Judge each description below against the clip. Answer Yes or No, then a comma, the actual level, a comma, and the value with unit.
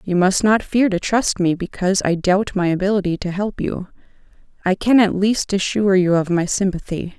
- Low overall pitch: No, high, 190 Hz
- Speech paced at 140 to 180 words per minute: No, average, 200 wpm